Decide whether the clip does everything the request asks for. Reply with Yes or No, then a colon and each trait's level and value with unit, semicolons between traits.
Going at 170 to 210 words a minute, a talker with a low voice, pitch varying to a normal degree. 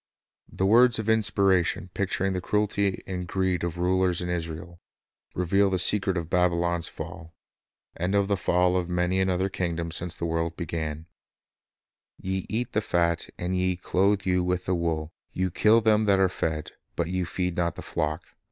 No: average, 180 wpm; very low, 90 Hz; narrow, 2.1 semitones